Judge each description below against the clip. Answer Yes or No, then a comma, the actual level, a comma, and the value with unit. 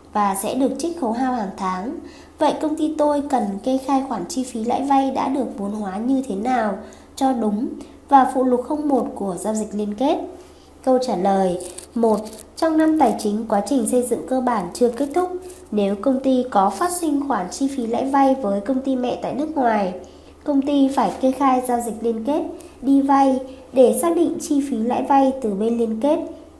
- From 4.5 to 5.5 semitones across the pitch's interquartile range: No, average, 3.9 semitones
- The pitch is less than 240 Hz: No, very high, 260 Hz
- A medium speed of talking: Yes, average, 215 wpm